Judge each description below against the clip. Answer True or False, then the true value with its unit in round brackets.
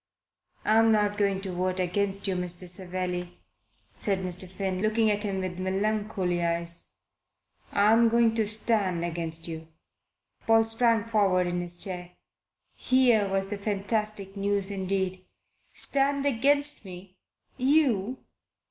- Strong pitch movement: False (3.3 semitones)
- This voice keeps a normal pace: False (130 wpm)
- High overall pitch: True (195 Hz)